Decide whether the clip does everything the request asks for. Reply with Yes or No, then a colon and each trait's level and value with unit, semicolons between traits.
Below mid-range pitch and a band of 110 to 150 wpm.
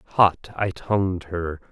Yes: very low, 90 Hz; average, 140 wpm